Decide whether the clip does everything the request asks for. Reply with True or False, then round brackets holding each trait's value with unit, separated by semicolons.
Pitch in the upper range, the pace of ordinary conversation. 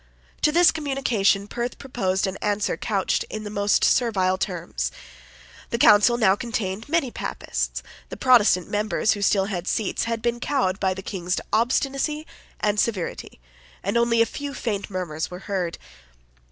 True (210 Hz; 155 wpm)